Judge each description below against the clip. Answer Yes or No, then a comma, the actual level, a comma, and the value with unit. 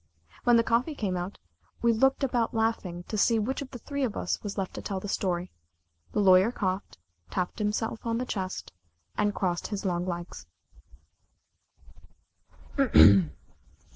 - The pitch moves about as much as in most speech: Yes, average, 3.9 semitones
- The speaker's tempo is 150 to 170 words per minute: Yes, average, 155 wpm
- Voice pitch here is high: Yes, high, 210 Hz